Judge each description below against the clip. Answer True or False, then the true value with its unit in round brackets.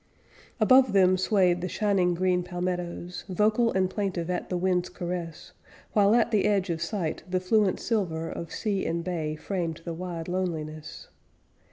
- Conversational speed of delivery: True (160 wpm)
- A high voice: False (180 Hz)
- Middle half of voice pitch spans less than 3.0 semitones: True (2.4 semitones)